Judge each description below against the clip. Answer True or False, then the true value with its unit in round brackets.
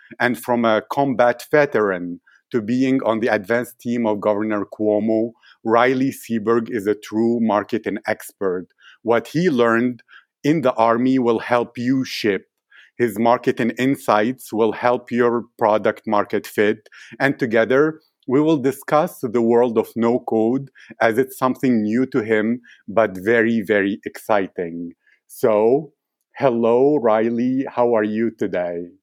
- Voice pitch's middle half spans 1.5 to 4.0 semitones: True (2.6 semitones)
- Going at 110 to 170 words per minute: True (140 wpm)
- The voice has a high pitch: False (120 Hz)